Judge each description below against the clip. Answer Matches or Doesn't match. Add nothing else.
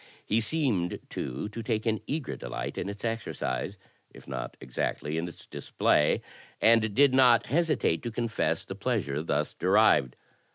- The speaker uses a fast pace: Doesn't match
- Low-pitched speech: Matches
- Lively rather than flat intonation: Matches